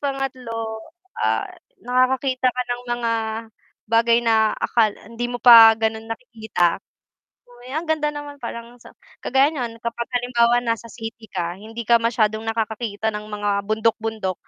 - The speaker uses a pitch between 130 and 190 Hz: No, high, 230 Hz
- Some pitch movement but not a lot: No, narrow, 2.0 semitones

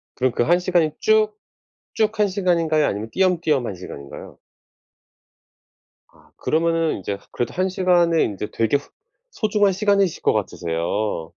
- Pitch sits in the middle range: Yes, medium, 165 Hz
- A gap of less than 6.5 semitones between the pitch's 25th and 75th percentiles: No, wide, 9.0 semitones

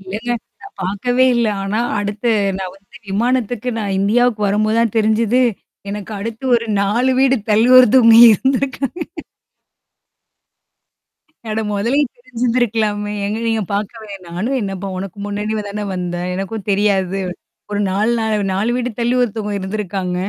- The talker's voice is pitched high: Yes, high, 215 Hz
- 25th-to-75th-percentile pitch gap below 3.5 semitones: Yes, average, 3.1 semitones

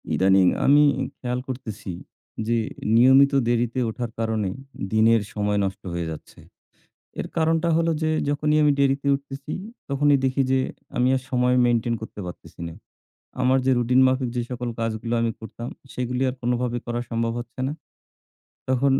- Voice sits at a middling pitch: No, low, 125 Hz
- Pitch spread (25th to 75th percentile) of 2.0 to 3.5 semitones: Yes, average, 2.9 semitones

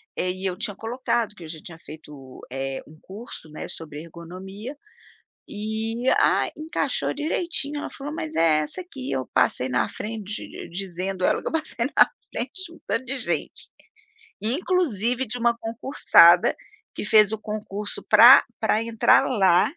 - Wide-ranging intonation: Yes, wide, 6.7 semitones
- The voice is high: Yes, high, 215 Hz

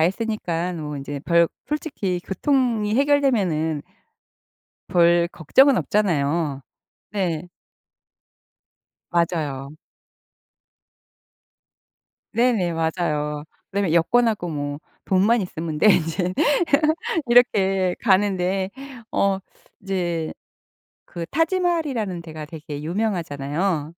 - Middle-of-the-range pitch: Yes, medium, 180 Hz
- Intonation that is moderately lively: Yes, average, 4.9 semitones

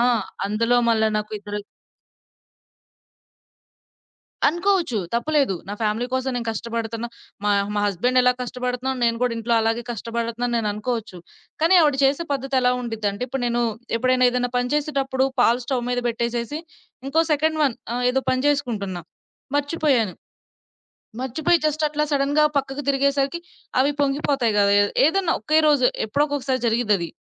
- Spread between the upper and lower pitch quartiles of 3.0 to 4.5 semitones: Yes, average, 3.5 semitones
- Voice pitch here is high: Yes, very high, 250 Hz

